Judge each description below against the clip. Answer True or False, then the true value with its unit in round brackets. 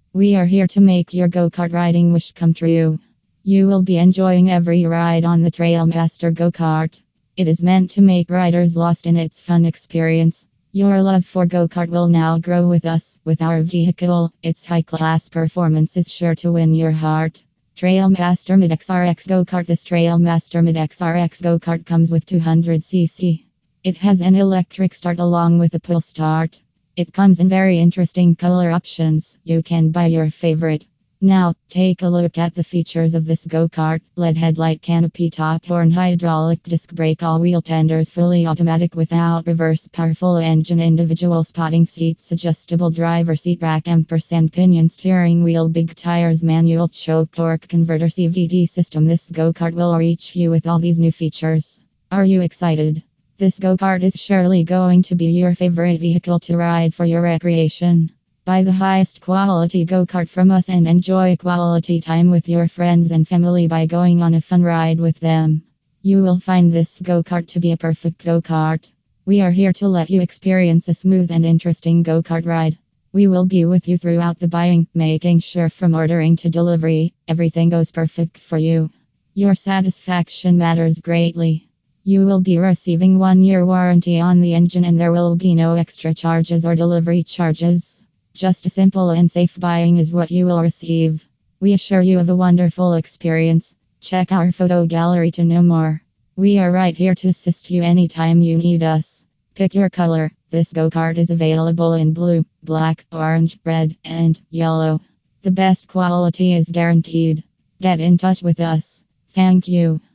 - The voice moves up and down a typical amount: False (1.5 semitones)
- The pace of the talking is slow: False (180 wpm)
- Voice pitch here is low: False (170 Hz)